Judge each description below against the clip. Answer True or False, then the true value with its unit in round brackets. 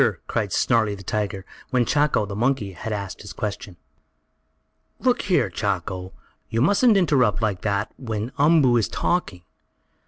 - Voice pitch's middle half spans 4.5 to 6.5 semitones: True (5.3 semitones)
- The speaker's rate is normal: True (145 wpm)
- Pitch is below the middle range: True (110 Hz)